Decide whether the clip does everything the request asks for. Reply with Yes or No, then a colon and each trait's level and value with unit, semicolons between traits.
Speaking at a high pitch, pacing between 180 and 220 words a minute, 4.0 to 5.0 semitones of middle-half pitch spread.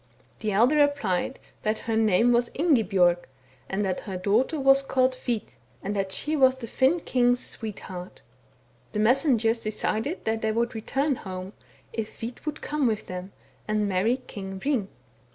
No: high, 225 Hz; average, 165 wpm; average, 4.5 semitones